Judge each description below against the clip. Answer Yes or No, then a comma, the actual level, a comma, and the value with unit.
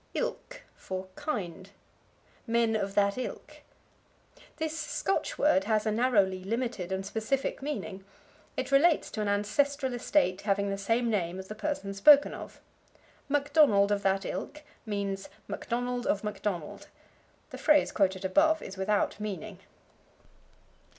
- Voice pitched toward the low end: No, high, 210 Hz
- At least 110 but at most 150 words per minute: Yes, slow, 135 wpm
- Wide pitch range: Yes, wide, 5.9 semitones